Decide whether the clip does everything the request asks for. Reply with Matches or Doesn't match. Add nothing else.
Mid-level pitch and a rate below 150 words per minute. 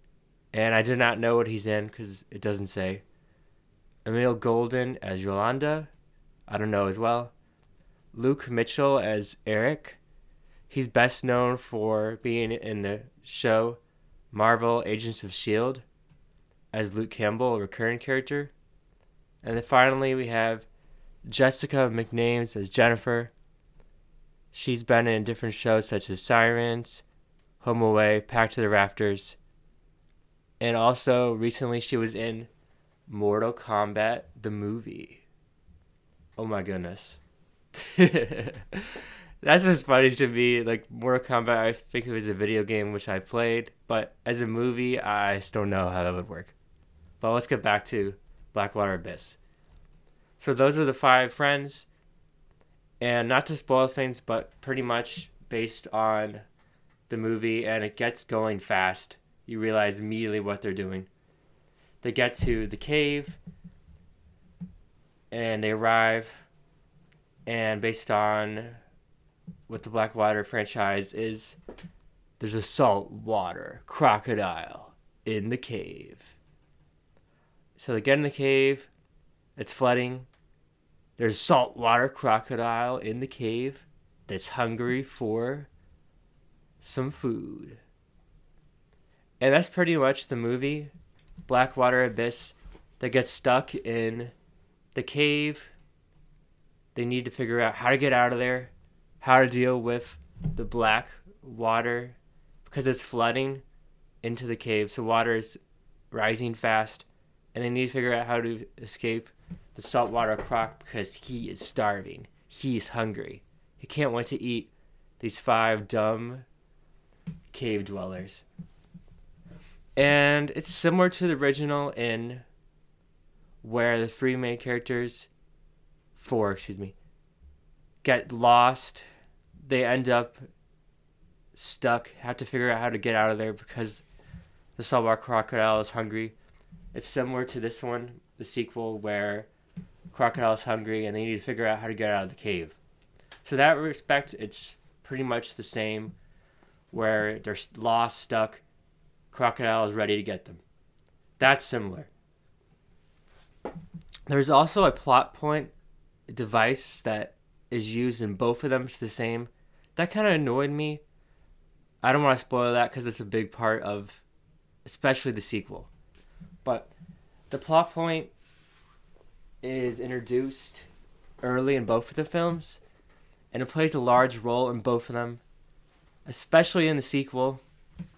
Doesn't match